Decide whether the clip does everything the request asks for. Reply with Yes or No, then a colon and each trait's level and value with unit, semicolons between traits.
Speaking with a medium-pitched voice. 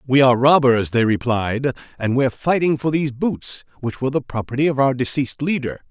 No: low, 130 Hz